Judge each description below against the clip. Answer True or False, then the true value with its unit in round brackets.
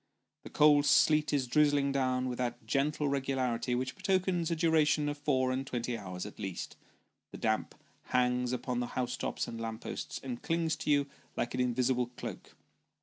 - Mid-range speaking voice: False (130 Hz)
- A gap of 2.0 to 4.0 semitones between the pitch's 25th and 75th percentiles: True (3.2 semitones)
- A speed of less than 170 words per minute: False (180 wpm)